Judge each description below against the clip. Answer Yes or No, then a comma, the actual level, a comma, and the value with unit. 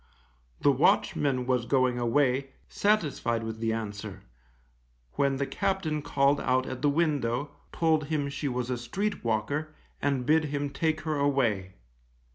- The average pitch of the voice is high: No, medium, 140 Hz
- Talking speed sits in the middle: Yes, average, 145 wpm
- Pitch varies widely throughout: No, average, 3.8 semitones